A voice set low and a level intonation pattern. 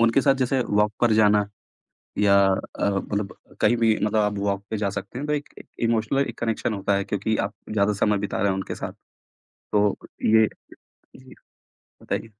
Yes: low, 105 Hz; narrow, 2.3 semitones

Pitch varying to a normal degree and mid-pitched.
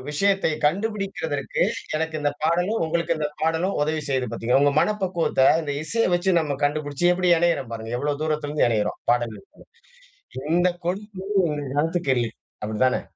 Yes: average, 3.9 semitones; medium, 155 Hz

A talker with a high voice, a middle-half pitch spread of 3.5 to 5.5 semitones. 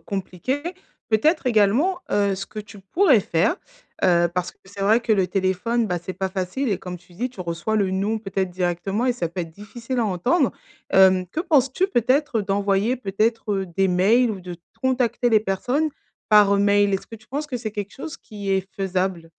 Yes: high, 205 Hz; average, 4.1 semitones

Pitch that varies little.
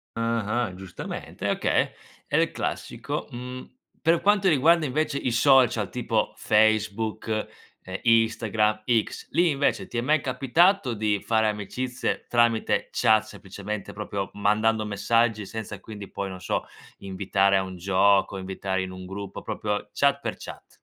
No: average, 3.9 semitones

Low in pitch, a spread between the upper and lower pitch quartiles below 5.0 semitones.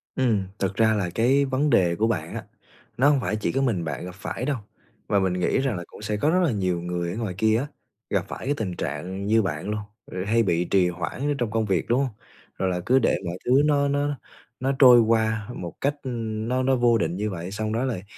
No: low, 110 Hz; wide, 5.6 semitones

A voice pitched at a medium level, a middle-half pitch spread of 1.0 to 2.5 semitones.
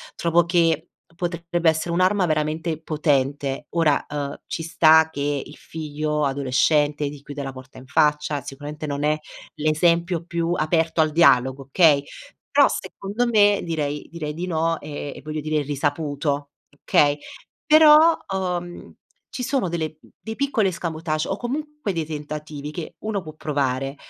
No: medium, 155 Hz; average, 2.9 semitones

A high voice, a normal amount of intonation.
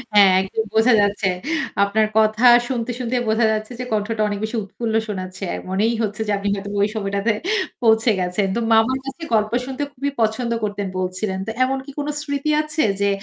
Yes: high, 220 Hz; average, 3.1 semitones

